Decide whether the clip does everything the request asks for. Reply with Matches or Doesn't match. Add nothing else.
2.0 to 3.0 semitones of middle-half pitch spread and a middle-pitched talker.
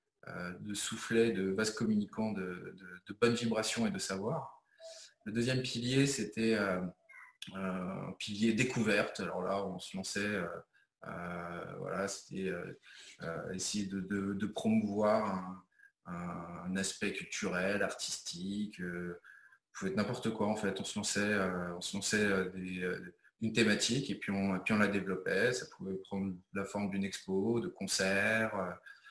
Doesn't match